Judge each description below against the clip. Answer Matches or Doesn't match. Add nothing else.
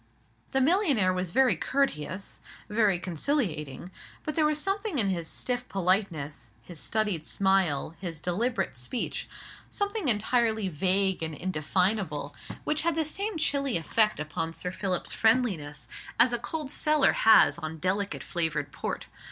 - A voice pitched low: Doesn't match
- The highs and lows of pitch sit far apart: Matches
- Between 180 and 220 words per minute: Doesn't match